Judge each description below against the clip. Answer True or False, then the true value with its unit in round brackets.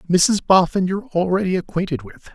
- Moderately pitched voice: True (180 Hz)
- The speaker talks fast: False (155 wpm)